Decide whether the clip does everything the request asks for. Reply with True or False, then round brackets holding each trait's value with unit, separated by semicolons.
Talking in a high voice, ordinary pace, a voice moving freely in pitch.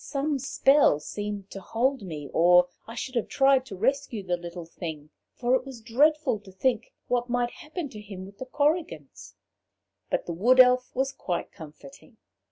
True (230 Hz; 175 wpm; 6.6 semitones)